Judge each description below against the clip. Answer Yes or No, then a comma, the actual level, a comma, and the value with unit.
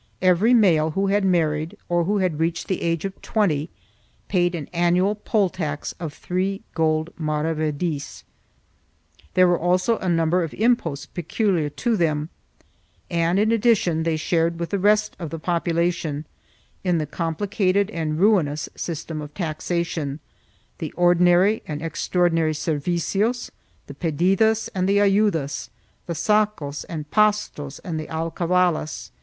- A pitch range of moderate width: Yes, average, 3.6 semitones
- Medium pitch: Yes, medium, 170 Hz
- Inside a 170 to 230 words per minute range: No, average, 145 wpm